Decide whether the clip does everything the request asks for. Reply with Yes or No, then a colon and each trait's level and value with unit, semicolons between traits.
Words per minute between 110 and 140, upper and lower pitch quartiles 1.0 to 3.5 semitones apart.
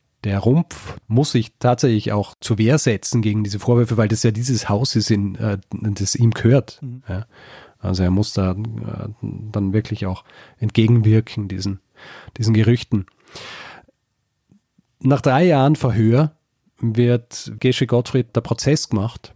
Yes: average, 130 wpm; average, 2.8 semitones